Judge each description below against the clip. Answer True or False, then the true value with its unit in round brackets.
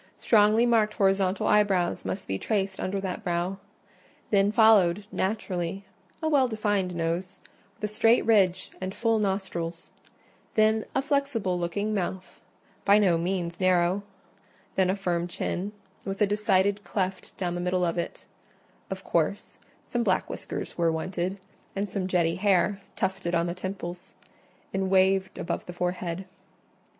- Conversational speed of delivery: True (145 wpm)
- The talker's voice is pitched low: False (190 Hz)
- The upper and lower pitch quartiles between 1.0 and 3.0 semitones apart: True (2.6 semitones)